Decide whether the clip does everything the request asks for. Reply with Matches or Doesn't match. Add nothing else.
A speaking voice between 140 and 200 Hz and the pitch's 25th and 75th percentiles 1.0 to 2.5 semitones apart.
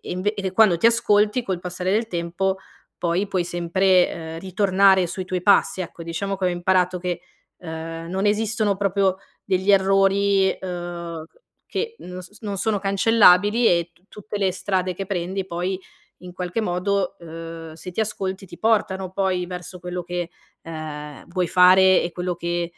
Matches